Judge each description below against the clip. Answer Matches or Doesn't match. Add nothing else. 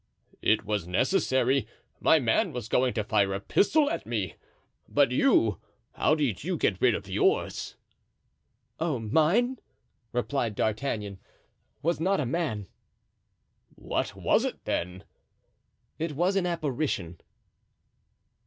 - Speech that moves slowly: Matches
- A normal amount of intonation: Doesn't match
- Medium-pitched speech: Doesn't match